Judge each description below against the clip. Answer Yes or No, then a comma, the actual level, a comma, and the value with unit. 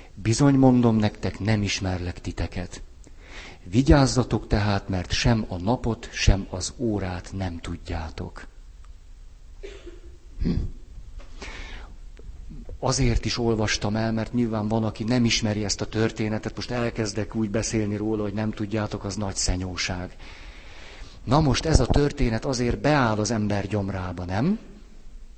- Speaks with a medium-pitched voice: No, low, 105 Hz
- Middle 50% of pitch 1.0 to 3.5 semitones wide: No, average, 4.0 semitones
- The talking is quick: No, average, 125 wpm